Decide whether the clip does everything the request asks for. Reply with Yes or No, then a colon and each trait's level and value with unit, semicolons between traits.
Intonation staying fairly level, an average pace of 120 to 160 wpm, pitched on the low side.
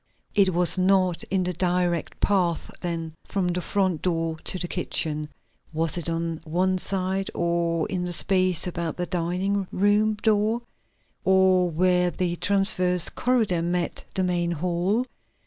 No: narrow, 1.9 semitones; average, 145 wpm; medium, 180 Hz